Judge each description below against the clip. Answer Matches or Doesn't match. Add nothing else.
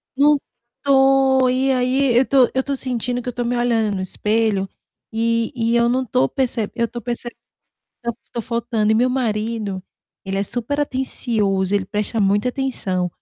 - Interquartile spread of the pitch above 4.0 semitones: Doesn't match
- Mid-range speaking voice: Doesn't match